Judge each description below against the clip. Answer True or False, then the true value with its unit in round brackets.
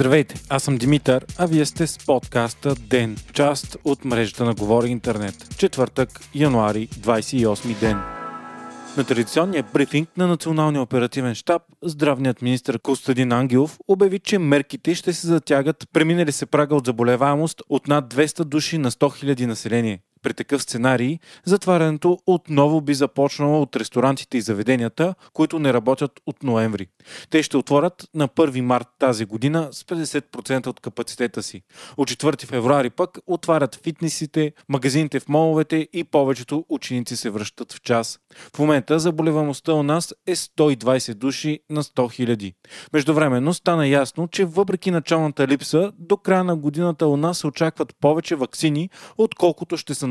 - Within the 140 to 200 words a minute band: True (150 wpm)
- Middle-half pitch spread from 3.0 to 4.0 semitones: False (4.4 semitones)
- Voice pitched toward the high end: False (145 Hz)